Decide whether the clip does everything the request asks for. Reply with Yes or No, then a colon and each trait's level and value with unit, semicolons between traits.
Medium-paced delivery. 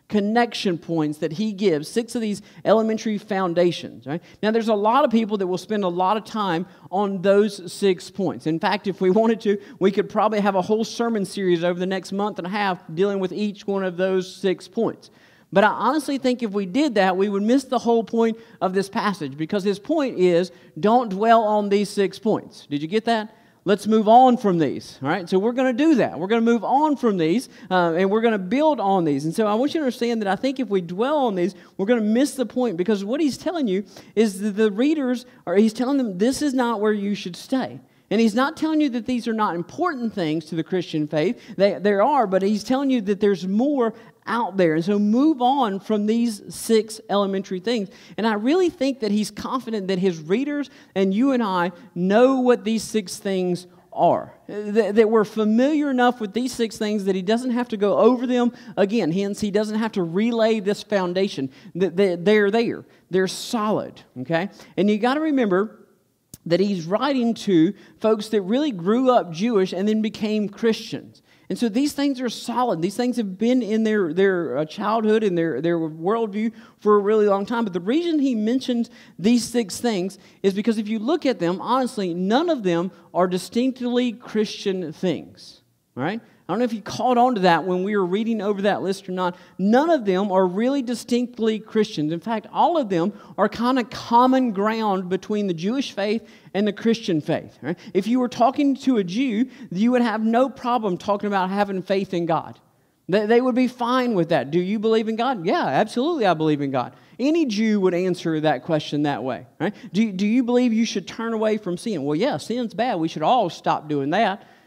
No: fast, 220 wpm